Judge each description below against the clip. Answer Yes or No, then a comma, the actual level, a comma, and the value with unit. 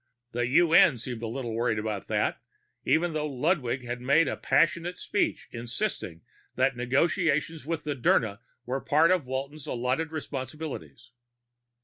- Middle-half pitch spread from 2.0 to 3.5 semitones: No, average, 4.9 semitones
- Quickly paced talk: No, slow, 135 wpm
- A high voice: No, low, 135 Hz